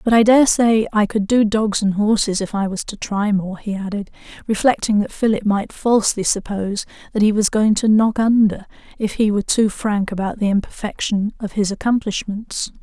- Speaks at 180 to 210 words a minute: Yes, average, 195 wpm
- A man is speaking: No, female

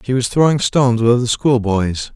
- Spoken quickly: No, average, 195 wpm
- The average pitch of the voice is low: Yes, low, 120 Hz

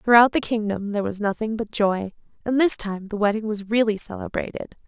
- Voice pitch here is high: Yes, high, 215 Hz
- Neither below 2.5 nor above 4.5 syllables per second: No, 5.6 syllables/s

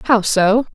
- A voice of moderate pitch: No, high, 220 Hz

